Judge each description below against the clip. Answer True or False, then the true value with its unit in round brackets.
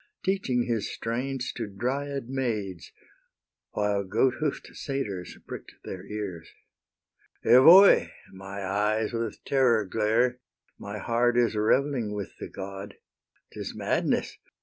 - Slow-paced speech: True (115 wpm)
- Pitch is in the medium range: False (115 Hz)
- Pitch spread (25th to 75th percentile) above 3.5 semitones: True (4.3 semitones)